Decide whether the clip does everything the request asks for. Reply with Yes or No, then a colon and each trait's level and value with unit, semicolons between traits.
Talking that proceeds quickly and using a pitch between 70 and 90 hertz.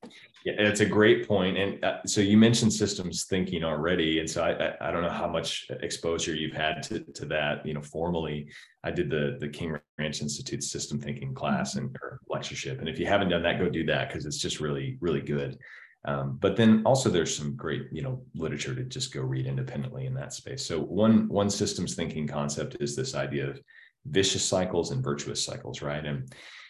Yes: fast, 210 wpm; very low, 80 Hz